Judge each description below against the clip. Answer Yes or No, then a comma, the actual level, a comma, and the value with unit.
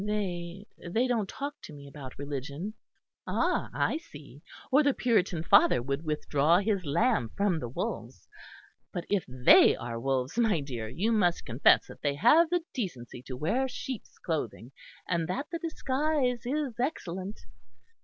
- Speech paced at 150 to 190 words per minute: Yes, average, 155 wpm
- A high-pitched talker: No, medium, 180 Hz